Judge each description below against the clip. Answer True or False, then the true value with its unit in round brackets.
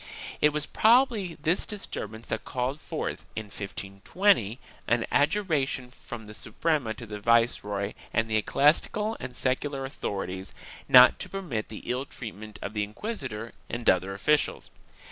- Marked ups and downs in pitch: True (6.0 semitones)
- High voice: False (120 Hz)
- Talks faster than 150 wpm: False (145 wpm)